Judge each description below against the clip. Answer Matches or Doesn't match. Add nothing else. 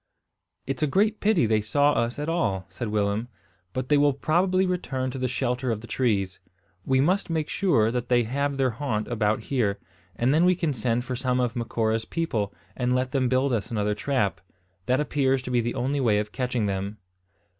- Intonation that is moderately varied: Matches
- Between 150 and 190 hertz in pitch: Doesn't match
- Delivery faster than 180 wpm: Matches